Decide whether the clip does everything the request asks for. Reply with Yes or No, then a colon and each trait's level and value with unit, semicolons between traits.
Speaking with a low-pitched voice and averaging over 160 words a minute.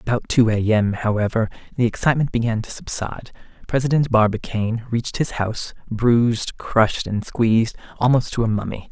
No: low, 115 Hz; average, 155 wpm